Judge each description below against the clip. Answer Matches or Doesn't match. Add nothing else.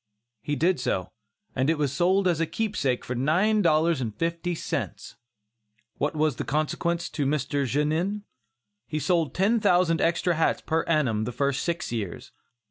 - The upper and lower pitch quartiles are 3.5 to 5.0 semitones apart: Matches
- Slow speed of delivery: Doesn't match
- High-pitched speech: Doesn't match